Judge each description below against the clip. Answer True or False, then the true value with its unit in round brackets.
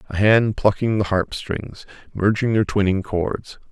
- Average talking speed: True (145 wpm)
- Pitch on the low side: True (100 Hz)